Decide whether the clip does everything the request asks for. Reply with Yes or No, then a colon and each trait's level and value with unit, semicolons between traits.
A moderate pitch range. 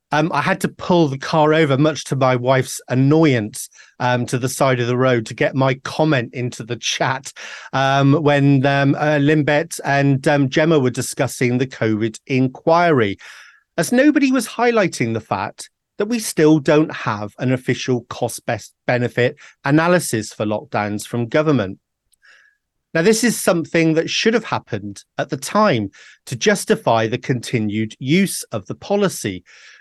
Yes: average, 4.7 semitones